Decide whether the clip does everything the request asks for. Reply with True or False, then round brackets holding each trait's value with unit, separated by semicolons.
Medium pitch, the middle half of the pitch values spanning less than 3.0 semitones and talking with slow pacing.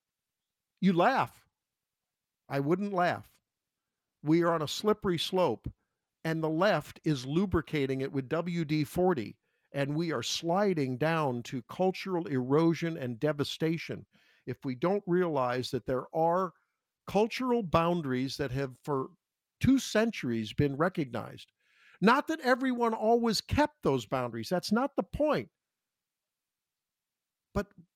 False (165 Hz; 5.5 semitones; 125 wpm)